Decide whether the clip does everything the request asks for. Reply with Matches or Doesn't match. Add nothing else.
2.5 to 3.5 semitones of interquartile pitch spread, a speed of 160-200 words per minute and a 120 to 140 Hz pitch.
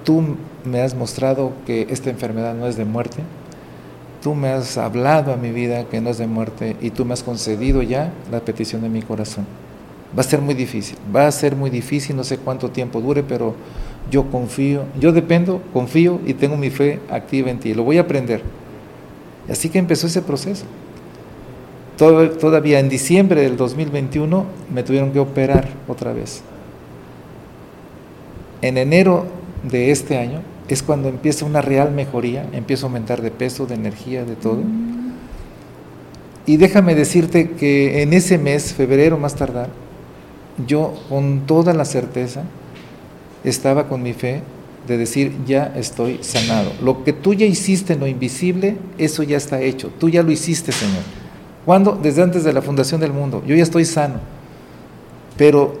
Doesn't match